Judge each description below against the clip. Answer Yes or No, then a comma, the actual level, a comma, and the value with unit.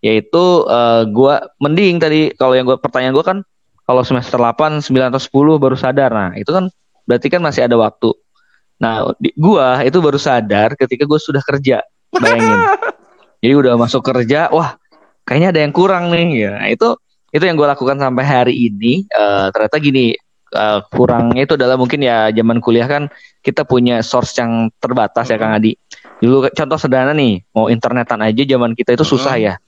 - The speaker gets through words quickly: Yes, fast, 185 wpm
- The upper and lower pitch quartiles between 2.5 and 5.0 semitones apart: Yes, average, 3.5 semitones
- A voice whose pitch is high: No, low, 130 Hz